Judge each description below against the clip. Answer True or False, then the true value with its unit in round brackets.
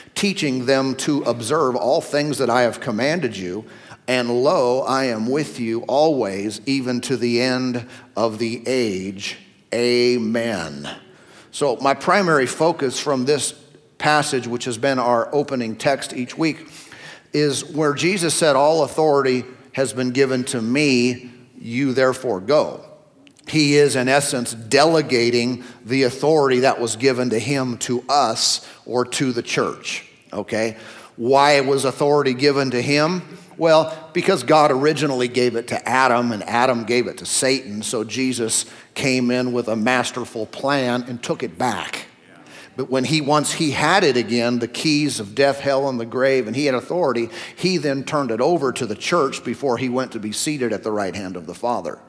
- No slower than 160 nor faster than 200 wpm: True (170 wpm)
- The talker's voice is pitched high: False (130 Hz)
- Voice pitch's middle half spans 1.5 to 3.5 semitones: True (3.1 semitones)